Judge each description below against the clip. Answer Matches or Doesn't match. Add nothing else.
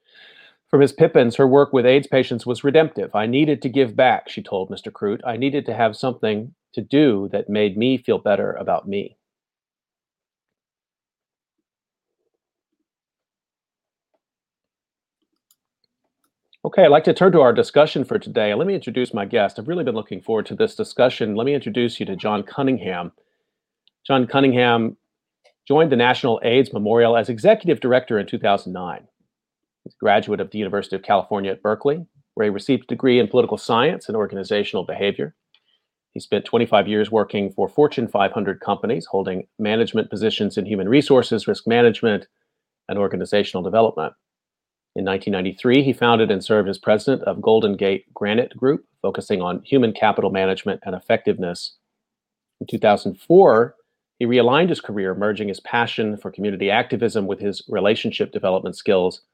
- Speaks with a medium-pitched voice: Doesn't match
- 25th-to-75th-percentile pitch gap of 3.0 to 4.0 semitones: Doesn't match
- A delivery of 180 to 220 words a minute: Doesn't match